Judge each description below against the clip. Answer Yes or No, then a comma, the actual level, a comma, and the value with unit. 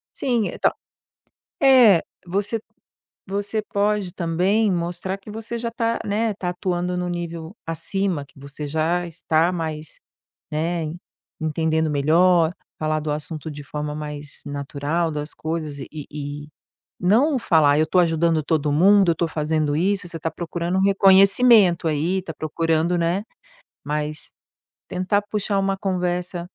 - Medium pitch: Yes, medium, 170 Hz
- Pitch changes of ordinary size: Yes, average, 3.9 semitones